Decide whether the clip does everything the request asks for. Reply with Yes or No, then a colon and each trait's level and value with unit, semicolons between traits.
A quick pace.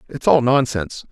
No: average, 160 wpm